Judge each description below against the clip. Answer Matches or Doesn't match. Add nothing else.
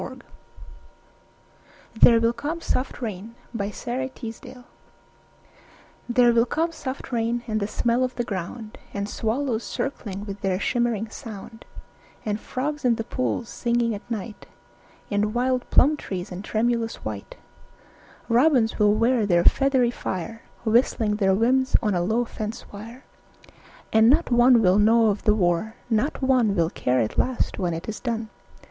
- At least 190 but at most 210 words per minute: Doesn't match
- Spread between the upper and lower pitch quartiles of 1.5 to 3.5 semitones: Matches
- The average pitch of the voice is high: Matches